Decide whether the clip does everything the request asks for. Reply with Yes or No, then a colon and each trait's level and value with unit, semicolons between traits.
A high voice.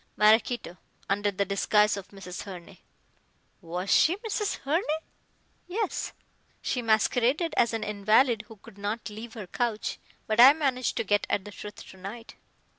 Yes: high, 215 Hz